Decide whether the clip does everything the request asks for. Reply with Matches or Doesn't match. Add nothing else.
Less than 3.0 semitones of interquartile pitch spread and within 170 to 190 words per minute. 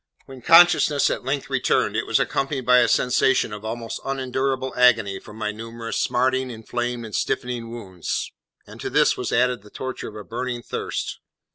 Matches